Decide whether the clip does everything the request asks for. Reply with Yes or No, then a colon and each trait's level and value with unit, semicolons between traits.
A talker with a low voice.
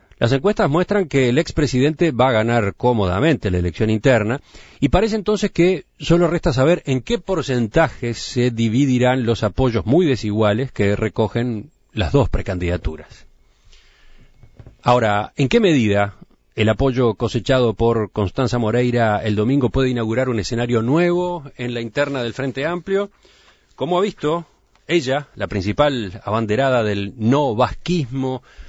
Yes: low, 125 Hz